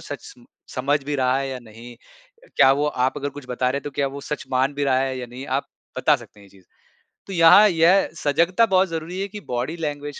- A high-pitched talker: No, medium, 145 Hz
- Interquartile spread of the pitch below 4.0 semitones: No, average, 4.3 semitones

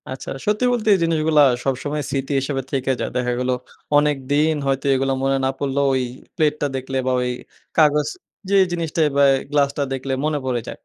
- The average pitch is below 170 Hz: Yes, medium, 140 Hz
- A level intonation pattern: Yes, narrow, 2.3 semitones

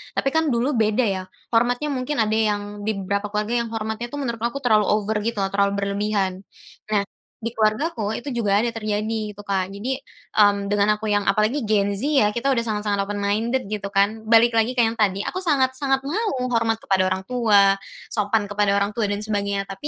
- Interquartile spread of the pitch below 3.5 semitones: Yes, average, 2.7 semitones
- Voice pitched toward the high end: Yes, high, 215 Hz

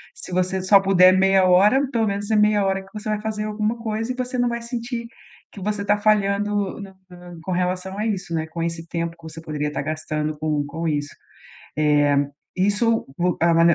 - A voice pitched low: No, high, 190 Hz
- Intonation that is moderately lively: Yes, average, 4.0 semitones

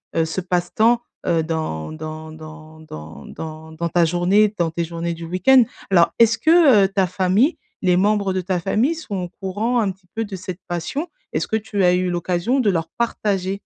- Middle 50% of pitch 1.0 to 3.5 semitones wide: No, average, 4.0 semitones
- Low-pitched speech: No, medium, 185 Hz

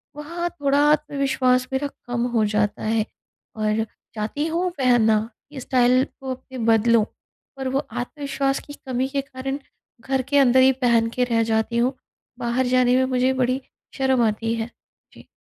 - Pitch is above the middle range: Yes, very high, 255 Hz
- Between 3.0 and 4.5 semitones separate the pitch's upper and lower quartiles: No, narrow, 2.6 semitones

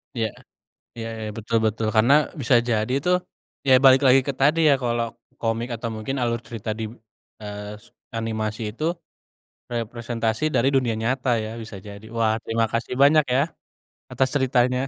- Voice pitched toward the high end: No, low, 115 Hz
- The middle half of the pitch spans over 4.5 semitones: No, average, 2.8 semitones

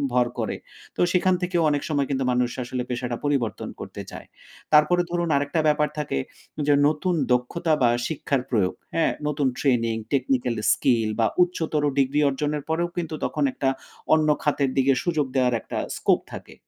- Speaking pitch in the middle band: Yes, medium, 145 Hz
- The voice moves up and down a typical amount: Yes, average, 3.9 semitones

